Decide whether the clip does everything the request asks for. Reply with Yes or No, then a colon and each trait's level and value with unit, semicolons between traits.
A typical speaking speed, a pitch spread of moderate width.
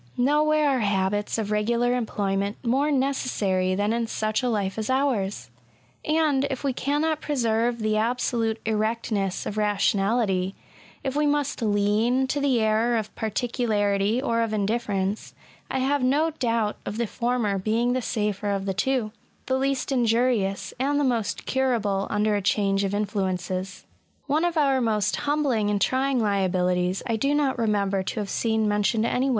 Yes: average, 170 wpm; average, 4.3 semitones